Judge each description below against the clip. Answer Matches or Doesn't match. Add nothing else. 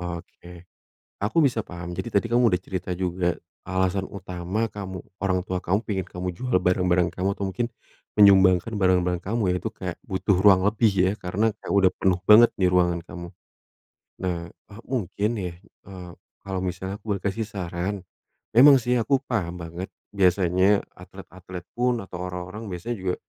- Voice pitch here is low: Matches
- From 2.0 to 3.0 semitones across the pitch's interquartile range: Matches